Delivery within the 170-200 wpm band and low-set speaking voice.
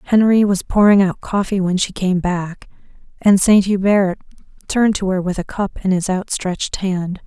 No: average, 180 wpm; high, 190 Hz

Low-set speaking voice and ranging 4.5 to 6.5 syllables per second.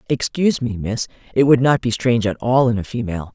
Yes: low, 120 Hz; 6.3 syllables/s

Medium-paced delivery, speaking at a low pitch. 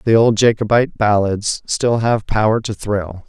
Yes: average, 165 wpm; low, 110 Hz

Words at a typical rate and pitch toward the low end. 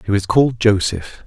Yes: average, 190 wpm; low, 105 Hz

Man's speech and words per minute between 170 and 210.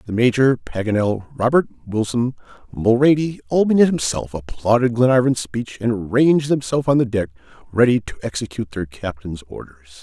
No: male; average, 140 wpm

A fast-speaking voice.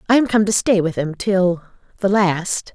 No: average, 195 wpm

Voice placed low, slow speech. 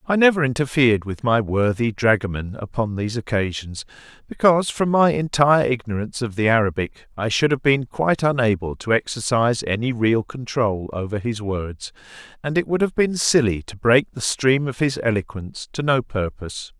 No: low, 120 Hz; average, 170 wpm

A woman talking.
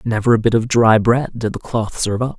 No: male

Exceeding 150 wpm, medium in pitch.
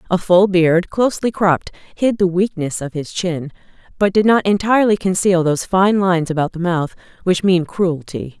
Yes: average, 180 wpm; medium, 180 Hz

